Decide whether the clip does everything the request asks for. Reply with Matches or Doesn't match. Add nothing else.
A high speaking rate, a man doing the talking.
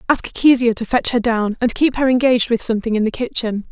Doesn't match